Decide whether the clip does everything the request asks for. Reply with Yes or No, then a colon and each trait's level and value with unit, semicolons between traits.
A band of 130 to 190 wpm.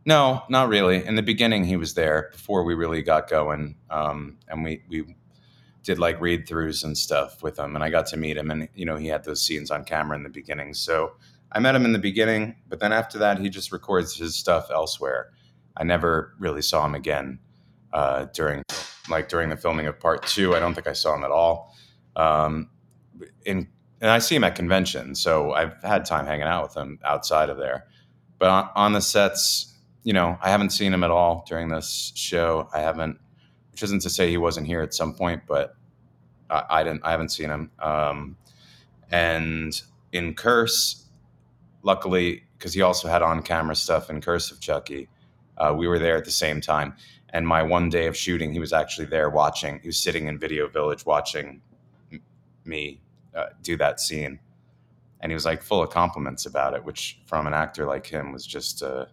No: fast, 205 wpm